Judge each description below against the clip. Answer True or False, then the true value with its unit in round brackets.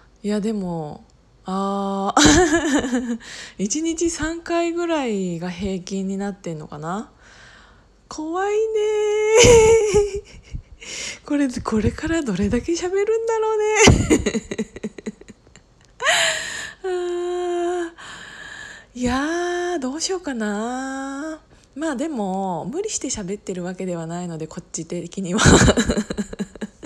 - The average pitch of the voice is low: False (265 Hz)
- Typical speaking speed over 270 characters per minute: False (180 characters per minute)